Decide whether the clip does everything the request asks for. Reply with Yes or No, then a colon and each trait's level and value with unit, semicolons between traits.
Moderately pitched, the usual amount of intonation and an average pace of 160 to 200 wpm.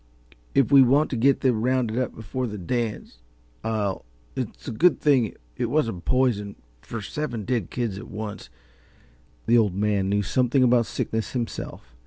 No: low, 115 Hz; average, 3.8 semitones; average, 170 wpm